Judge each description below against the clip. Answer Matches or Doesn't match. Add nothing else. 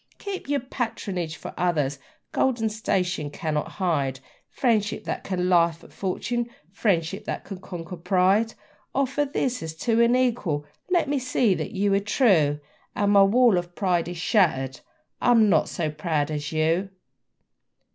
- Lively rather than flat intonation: Matches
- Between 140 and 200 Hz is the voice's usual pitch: Matches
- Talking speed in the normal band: Matches